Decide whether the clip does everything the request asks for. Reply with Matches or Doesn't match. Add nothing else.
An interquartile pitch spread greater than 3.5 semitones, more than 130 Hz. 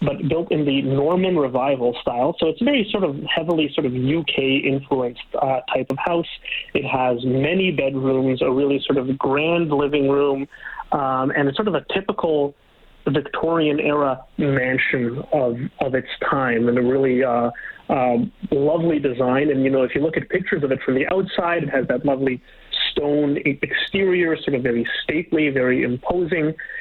Doesn't match